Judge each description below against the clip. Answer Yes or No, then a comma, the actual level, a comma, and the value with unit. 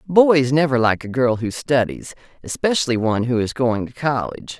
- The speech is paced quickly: No, average, 185 wpm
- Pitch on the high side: No, low, 130 Hz